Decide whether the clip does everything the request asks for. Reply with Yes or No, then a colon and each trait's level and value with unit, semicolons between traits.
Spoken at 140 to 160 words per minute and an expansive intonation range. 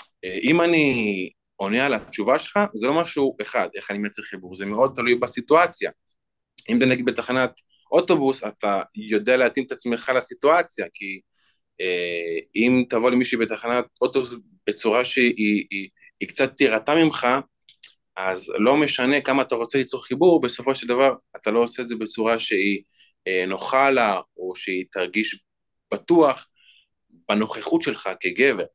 No: fast, 150 wpm; average, 4.5 semitones